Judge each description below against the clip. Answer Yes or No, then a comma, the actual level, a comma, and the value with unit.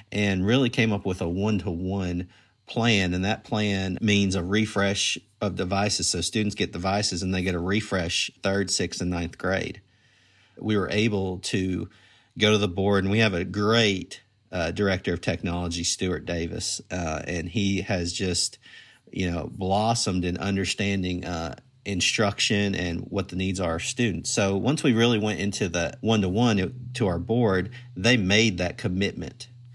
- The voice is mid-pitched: No, low, 100 Hz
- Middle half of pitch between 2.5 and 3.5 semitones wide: Yes, average, 2.8 semitones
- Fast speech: No, average, 165 wpm